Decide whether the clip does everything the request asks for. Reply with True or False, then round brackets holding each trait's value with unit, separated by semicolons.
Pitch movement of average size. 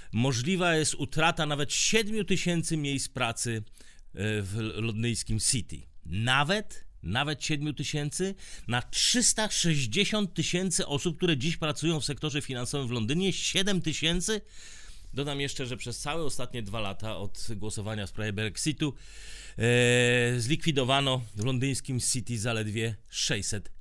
False (6.0 semitones)